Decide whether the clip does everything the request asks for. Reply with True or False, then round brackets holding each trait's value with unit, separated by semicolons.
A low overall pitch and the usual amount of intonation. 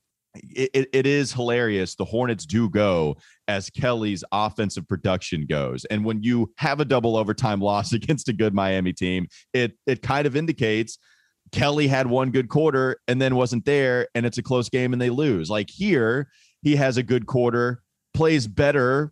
True (125 Hz; 3.8 semitones)